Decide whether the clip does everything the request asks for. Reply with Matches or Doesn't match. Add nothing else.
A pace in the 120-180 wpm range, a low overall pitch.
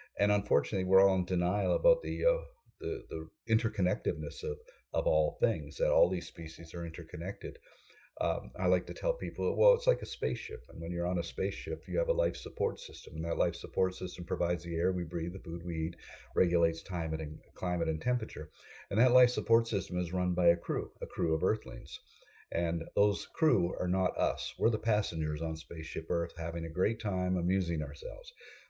Doesn't match